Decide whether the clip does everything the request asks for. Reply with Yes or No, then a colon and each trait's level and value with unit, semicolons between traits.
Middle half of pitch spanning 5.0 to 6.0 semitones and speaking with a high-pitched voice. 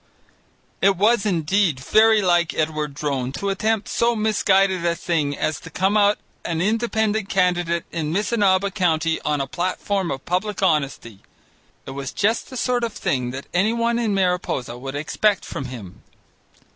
No: wide, 5.6 semitones; medium, 180 Hz